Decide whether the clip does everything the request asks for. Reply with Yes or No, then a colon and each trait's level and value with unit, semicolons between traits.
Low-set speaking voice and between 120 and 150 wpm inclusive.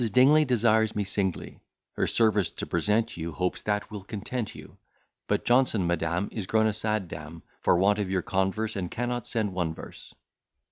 No: low, 105 Hz; average, 180 wpm